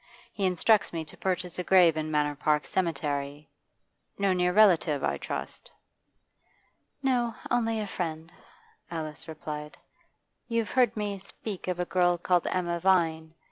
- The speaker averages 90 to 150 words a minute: Yes, average, 140 wpm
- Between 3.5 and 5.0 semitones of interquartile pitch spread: Yes, average, 3.9 semitones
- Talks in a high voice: No, medium, 175 Hz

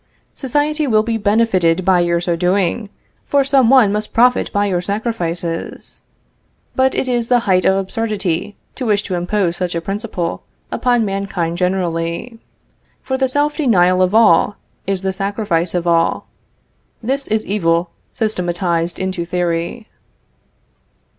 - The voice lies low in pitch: No, high, 195 Hz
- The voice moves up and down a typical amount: Yes, average, 4.6 semitones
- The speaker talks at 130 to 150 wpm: Yes, average, 140 wpm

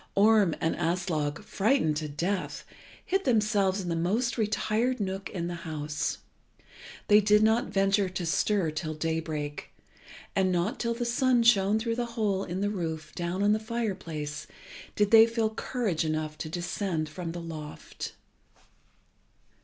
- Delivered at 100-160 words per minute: Yes, average, 155 wpm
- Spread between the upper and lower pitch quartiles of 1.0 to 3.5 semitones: No, average, 5.0 semitones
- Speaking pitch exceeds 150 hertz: Yes, high, 190 Hz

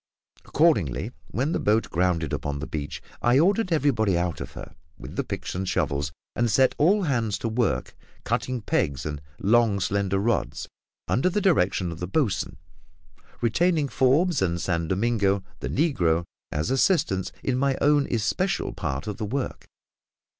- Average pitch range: No, wide, 7.6 semitones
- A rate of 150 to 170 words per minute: Yes, average, 160 wpm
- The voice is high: No, low, 110 Hz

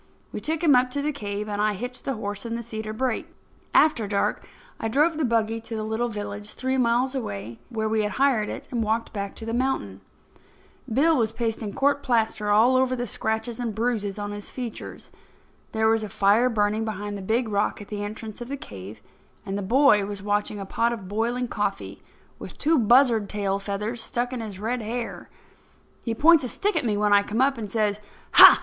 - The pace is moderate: No, fast, 210 wpm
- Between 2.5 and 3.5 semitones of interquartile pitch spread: Yes, average, 3.2 semitones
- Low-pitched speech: No, high, 225 Hz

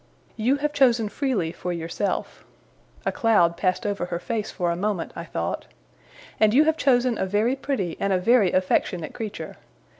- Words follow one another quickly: No, average, 175 wpm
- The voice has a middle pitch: No, high, 205 Hz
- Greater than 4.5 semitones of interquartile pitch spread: Yes, wide, 5.5 semitones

